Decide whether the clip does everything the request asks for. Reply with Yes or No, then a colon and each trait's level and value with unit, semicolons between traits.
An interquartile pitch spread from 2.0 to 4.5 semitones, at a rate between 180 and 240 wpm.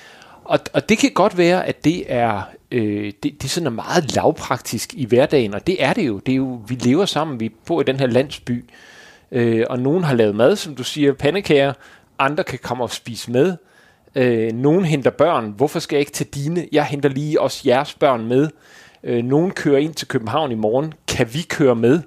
Yes: average, 4.0 semitones; average, 220 wpm